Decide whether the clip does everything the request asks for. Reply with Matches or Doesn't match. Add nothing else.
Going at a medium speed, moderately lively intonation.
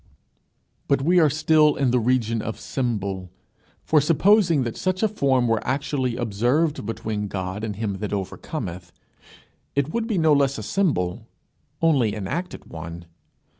Doesn't match